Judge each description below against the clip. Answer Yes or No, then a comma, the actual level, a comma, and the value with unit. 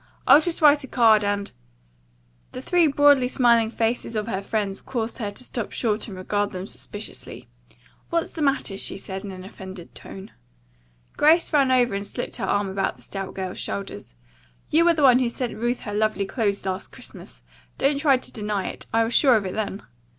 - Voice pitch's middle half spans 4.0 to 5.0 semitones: Yes, average, 4.7 semitones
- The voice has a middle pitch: No, high, 220 Hz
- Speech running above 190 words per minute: Yes, average, 200 wpm